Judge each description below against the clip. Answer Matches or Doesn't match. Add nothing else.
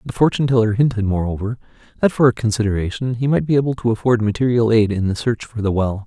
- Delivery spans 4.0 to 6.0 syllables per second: Doesn't match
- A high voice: Doesn't match